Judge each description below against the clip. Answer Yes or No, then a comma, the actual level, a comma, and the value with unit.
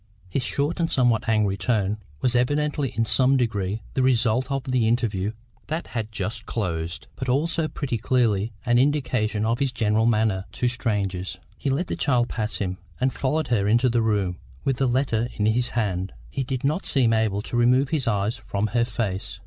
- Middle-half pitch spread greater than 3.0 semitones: Yes, average, 3.7 semitones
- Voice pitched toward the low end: Yes, low, 115 Hz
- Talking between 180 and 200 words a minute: Yes, average, 190 wpm